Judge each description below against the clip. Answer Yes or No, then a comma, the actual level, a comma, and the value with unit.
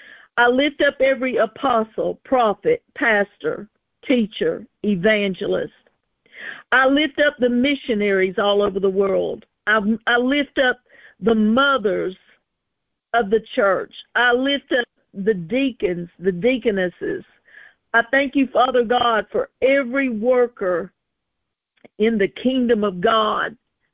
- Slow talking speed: Yes, slow, 120 wpm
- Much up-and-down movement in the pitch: No, average, 4.2 semitones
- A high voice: Yes, high, 240 Hz